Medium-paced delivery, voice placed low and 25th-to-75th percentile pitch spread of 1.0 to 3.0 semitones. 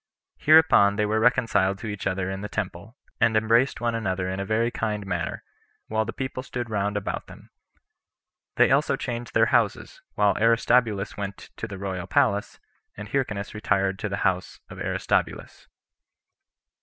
Yes: average, 165 wpm; low, 105 Hz; average, 2.7 semitones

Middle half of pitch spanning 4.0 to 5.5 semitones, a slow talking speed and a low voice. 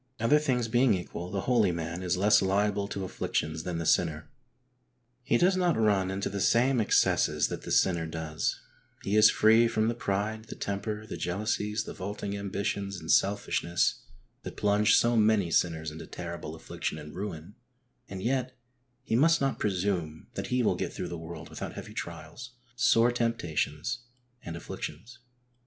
No: average, 4.8 semitones; average, 170 wpm; low, 100 Hz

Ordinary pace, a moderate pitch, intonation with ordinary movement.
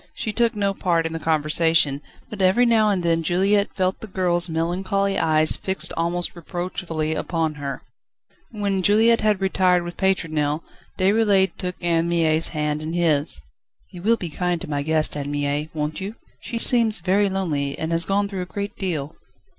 Yes: average, 180 wpm; medium, 175 Hz; average, 3.7 semitones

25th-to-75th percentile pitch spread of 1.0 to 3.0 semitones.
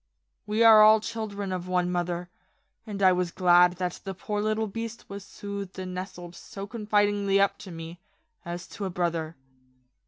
Yes: average, 2.7 semitones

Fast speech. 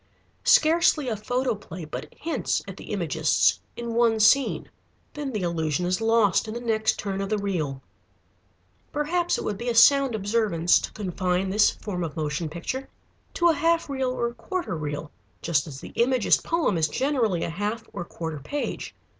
No: average, 175 wpm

